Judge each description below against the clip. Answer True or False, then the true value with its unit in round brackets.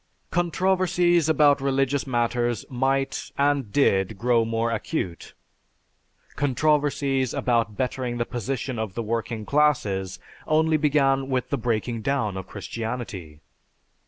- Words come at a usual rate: False (115 wpm)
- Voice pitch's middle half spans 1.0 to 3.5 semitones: False (4.0 semitones)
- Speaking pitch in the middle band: False (130 Hz)